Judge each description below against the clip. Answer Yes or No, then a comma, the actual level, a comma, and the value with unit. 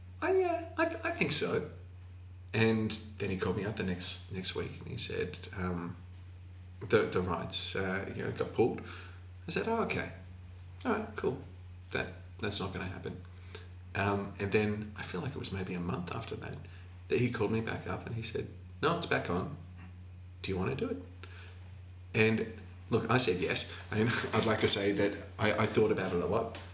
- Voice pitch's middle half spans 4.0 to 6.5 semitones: No, average, 2.8 semitones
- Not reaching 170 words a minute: No, fast, 205 wpm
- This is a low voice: Yes, very low, 90 Hz